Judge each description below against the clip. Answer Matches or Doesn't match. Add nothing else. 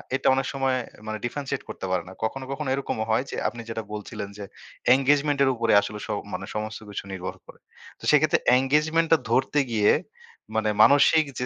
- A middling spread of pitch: Matches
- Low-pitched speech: Matches